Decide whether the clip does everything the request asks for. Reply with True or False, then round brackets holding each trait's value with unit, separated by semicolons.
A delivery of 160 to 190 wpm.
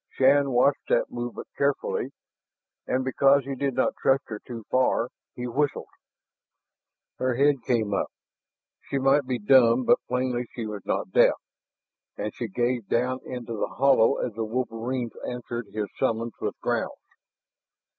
False (150 wpm)